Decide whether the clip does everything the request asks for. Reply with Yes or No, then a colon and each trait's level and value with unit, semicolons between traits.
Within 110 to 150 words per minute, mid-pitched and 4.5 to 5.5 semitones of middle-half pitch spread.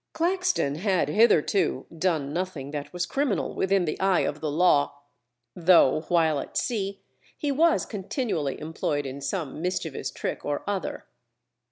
Yes: average, 145 wpm; medium, 175 Hz; average, 4.9 semitones